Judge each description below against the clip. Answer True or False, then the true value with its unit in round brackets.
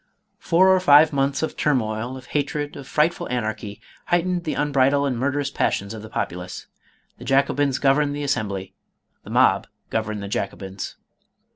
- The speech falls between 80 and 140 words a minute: False (160 wpm)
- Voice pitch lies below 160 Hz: True (135 Hz)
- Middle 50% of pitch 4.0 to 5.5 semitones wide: True (5.2 semitones)